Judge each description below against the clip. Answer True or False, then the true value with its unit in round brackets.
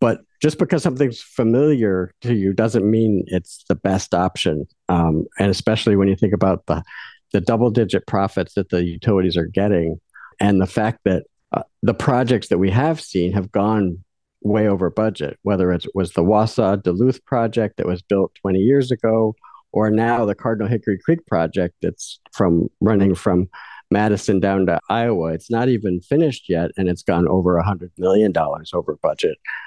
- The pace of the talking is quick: False (175 wpm)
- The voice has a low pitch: True (100 Hz)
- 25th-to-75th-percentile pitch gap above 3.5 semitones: True (4.1 semitones)